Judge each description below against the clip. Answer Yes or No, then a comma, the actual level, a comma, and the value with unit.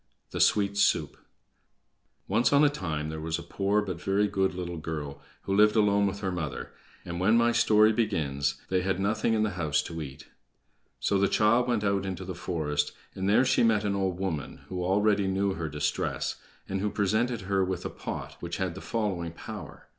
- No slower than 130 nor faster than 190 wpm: No, average, 200 wpm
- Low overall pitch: Yes, very low, 95 Hz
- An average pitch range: Yes, average, 3.5 semitones